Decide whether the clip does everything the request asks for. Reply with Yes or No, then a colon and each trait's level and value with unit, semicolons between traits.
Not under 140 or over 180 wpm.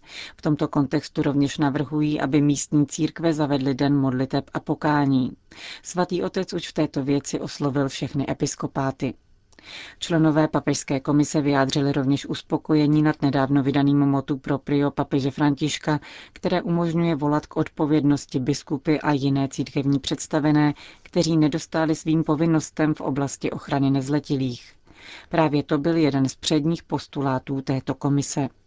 No: average, 130 wpm